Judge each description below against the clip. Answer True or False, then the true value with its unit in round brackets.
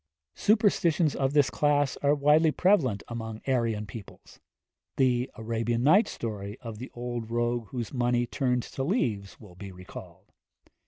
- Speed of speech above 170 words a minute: False (145 wpm)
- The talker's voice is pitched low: True (120 Hz)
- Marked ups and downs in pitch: False (4.3 semitones)